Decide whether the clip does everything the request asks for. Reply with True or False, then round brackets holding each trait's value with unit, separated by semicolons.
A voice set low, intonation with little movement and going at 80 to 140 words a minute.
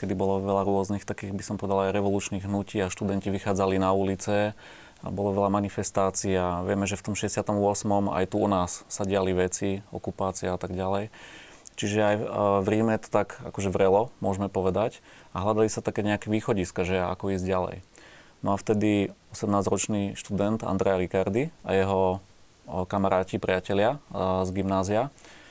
False (100 Hz; 1.5 semitones; 165 wpm)